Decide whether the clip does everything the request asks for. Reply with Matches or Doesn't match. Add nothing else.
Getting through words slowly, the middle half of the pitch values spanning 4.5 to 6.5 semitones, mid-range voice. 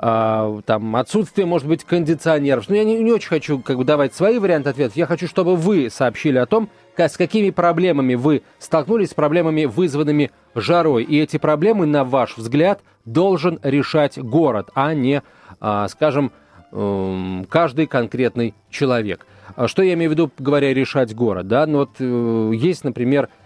Doesn't match